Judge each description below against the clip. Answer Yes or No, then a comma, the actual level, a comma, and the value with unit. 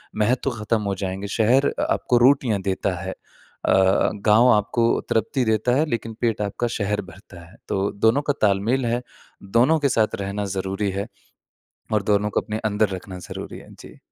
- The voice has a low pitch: Yes, low, 105 Hz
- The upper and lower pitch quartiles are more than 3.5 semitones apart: No, average, 3.2 semitones